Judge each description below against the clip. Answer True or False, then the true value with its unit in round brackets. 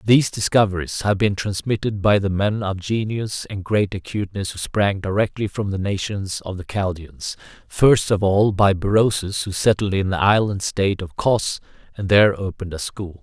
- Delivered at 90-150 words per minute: False (180 wpm)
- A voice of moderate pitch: False (100 Hz)